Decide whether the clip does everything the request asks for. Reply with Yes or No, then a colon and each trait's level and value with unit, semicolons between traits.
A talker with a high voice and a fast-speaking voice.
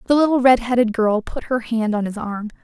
Yes: high, 230 Hz; fast, 250 wpm